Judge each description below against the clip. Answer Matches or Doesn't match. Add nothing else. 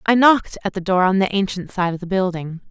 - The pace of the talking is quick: Matches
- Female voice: Matches